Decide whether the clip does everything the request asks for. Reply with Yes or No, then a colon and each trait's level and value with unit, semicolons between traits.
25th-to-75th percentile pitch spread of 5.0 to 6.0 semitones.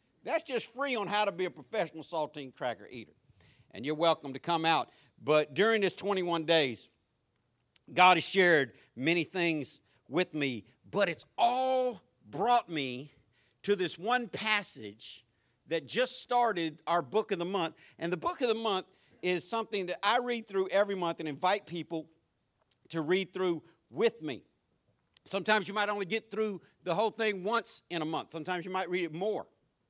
Yes: wide, 5.4 semitones